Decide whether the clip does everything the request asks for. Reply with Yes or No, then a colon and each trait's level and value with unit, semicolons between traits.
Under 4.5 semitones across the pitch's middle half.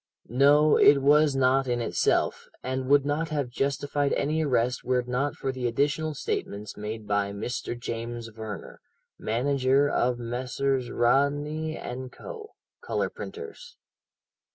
Yes: average, 3.2 semitones